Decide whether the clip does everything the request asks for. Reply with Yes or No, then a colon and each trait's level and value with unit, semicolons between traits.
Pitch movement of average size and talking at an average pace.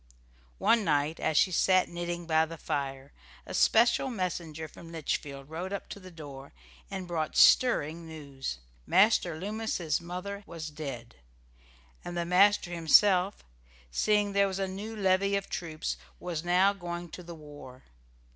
Yes: average, 3.7 semitones; average, 150 wpm